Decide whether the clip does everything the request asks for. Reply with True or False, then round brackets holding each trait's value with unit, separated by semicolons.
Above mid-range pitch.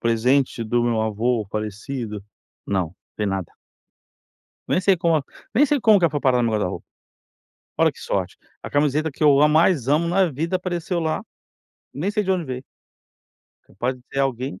False (135 Hz)